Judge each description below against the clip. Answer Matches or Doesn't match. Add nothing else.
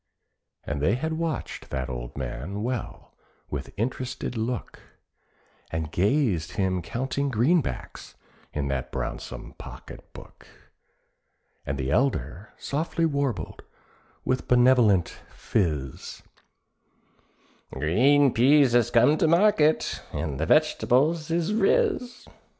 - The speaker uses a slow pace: Matches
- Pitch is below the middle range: Matches